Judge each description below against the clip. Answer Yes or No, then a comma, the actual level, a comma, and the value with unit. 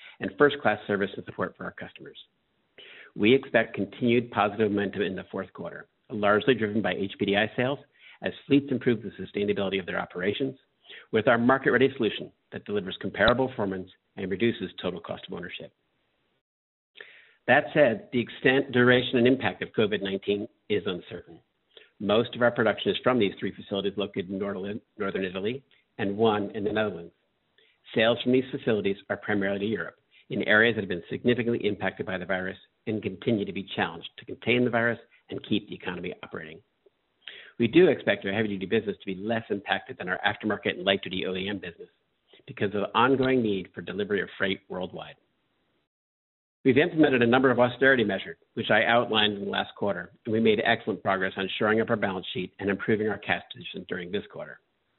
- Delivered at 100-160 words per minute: No, average, 185 wpm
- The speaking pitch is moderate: No, low, 110 Hz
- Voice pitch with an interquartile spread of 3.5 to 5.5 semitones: Yes, average, 3.8 semitones